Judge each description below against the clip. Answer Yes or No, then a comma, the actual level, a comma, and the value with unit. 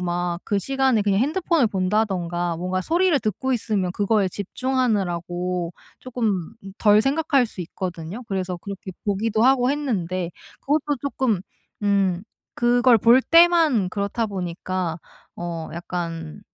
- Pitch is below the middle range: No, high, 200 Hz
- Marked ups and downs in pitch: Yes, wide, 5.8 semitones